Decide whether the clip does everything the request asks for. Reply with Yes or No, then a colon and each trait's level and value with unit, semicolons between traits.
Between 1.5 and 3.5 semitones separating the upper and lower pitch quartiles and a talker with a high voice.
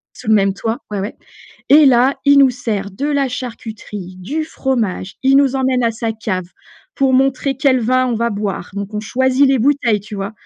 No: average, 4.3 semitones; high, 245 Hz